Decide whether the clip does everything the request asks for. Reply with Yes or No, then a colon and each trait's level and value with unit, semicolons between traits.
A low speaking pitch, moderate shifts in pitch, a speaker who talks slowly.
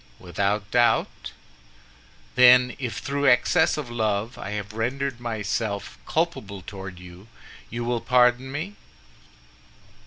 Yes: low, 120 Hz; average, 3.7 semitones; slow, 115 wpm